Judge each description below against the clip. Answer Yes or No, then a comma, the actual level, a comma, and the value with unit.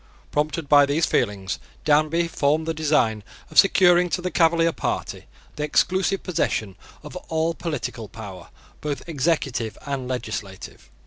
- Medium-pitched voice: Yes, medium, 150 Hz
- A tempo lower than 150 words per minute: Yes, slow, 135 wpm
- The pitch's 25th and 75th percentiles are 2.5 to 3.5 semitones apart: No, average, 4.8 semitones